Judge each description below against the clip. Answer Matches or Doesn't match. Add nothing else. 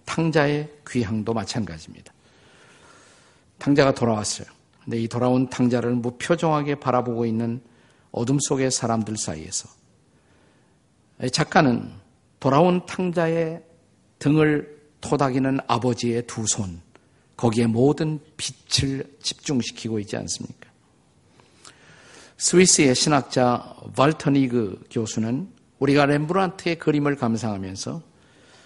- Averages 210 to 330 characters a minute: Matches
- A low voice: Matches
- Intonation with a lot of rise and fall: Doesn't match